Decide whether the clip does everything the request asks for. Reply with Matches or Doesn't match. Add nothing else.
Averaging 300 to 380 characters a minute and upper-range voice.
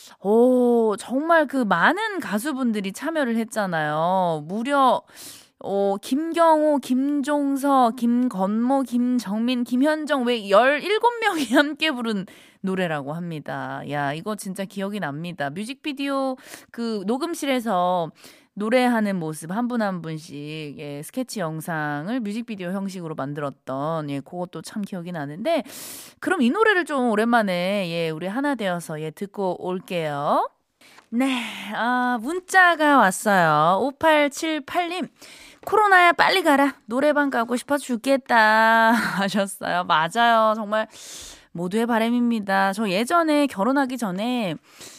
Doesn't match